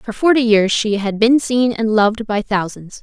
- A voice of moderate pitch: No, high, 220 Hz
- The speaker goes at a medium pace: No, fast, 220 wpm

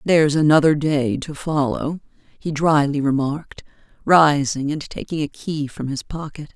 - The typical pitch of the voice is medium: Yes, medium, 150 Hz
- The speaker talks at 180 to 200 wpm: No, average, 145 wpm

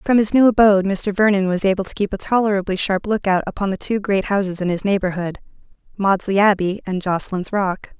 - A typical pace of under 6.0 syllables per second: No, 6.1 syllables/s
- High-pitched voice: Yes, high, 195 Hz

